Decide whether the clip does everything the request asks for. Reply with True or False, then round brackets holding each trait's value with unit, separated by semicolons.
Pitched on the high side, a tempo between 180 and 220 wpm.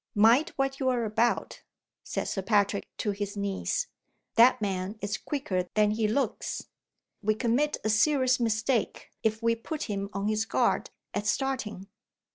False (220 Hz; 155 wpm)